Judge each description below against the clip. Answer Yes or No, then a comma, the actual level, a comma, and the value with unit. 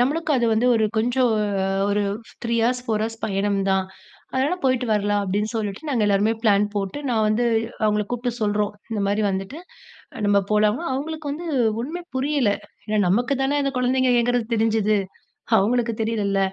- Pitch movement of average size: Yes, average, 3.4 semitones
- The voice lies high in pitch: Yes, high, 225 Hz